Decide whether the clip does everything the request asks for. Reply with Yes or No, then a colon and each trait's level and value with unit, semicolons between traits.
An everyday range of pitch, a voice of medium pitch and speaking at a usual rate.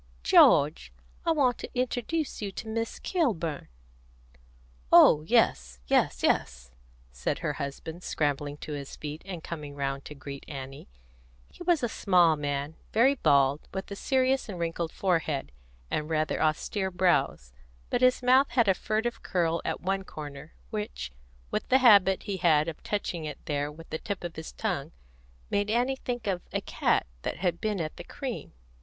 No: wide, 6.8 semitones; medium, 170 Hz; average, 170 wpm